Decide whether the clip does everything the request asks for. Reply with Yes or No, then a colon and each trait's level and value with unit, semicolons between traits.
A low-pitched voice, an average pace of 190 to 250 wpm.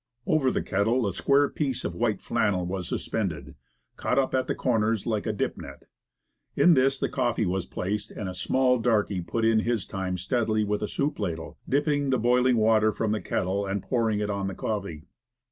Yes: low, 110 Hz; average, 200 wpm